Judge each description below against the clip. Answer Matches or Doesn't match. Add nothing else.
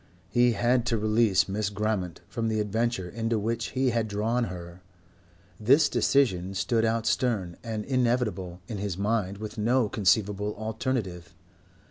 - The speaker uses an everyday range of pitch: Matches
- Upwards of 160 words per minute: Doesn't match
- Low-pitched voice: Matches